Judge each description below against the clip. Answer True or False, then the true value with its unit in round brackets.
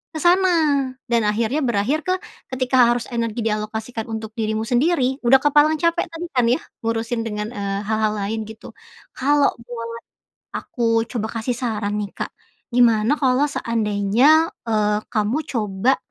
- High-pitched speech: True (235 Hz)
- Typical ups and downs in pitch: True (3.7 semitones)